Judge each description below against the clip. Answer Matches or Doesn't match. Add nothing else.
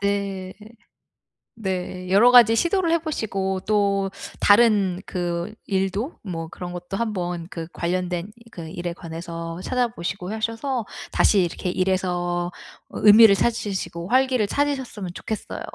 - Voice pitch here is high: Matches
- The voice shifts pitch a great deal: Doesn't match